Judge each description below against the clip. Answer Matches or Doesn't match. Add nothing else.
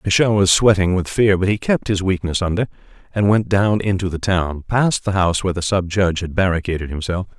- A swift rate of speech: Matches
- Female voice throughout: Doesn't match